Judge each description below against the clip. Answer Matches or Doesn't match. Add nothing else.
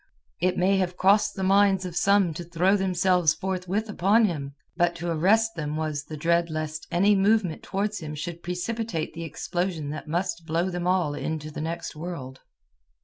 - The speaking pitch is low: Doesn't match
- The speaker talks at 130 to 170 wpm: Doesn't match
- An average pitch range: Matches